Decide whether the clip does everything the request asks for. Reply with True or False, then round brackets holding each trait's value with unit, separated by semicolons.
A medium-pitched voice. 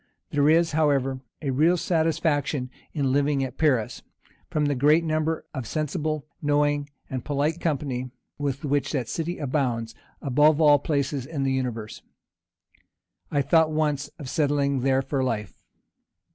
True (145 Hz)